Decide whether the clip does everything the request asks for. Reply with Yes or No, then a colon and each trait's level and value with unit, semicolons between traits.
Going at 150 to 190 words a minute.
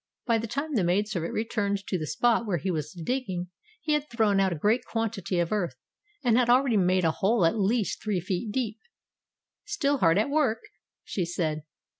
No: average, 200 wpm